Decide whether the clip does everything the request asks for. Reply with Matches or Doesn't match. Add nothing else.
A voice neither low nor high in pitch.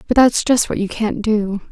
Doesn't match